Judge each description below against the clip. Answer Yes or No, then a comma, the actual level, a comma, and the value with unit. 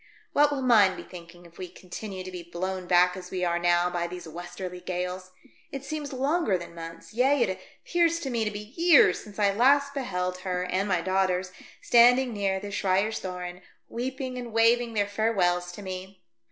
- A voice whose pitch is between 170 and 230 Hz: Yes, high, 190 Hz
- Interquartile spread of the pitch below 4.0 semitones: No, average, 4.9 semitones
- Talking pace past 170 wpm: Yes, average, 190 wpm